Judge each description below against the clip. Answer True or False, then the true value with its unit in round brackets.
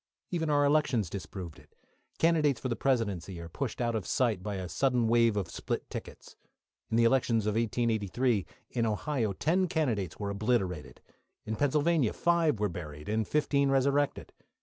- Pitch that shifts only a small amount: False (5.5 semitones)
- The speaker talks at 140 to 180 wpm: True (165 wpm)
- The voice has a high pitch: False (115 Hz)